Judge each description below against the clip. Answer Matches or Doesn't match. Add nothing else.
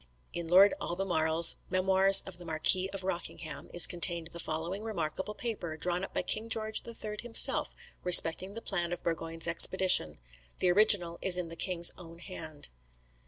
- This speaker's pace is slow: Doesn't match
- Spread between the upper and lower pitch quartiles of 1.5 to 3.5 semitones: Matches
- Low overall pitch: Doesn't match